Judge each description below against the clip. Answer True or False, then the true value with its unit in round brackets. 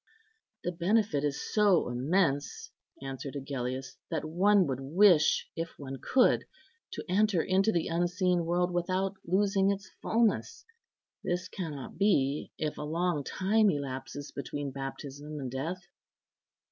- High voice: False (170 Hz)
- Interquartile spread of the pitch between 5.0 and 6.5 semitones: True (5.3 semitones)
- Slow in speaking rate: True (130 wpm)